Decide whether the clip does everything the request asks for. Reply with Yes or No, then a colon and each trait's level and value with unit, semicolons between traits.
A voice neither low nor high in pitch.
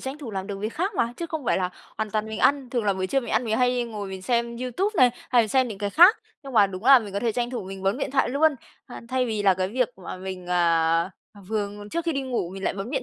No: high, 230 Hz